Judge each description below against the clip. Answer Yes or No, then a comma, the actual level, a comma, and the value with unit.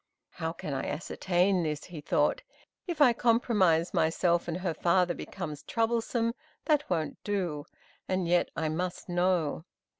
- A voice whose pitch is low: No, medium, 180 Hz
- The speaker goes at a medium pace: Yes, average, 145 wpm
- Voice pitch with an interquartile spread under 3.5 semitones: No, average, 4.1 semitones